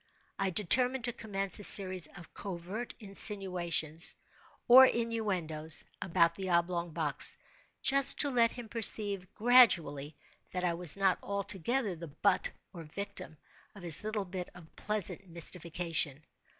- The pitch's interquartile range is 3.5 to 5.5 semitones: Yes, average, 4.0 semitones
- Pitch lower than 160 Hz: No, medium, 185 Hz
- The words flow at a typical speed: No, slow, 130 wpm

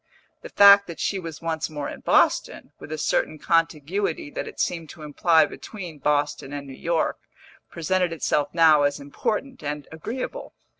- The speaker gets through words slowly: No, average, 165 wpm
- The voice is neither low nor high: Yes, medium, 160 Hz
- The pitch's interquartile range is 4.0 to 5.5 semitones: No, average, 3.3 semitones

